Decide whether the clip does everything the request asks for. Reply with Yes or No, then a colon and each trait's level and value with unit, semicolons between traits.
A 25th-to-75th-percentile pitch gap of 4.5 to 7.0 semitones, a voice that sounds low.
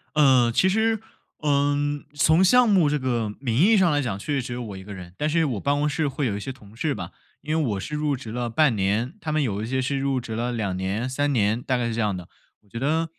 Yes: average, 4.8 semitones; low, 130 Hz